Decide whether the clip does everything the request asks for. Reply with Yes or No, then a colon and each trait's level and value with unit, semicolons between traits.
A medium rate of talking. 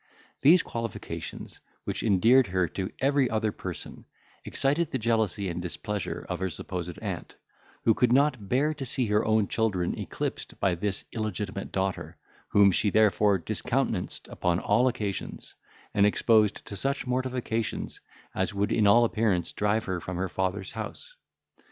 Yes: average, 150 wpm